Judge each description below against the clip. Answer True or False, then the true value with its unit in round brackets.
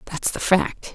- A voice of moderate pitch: True (175 Hz)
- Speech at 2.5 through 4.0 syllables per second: True (3.8 syllables/s)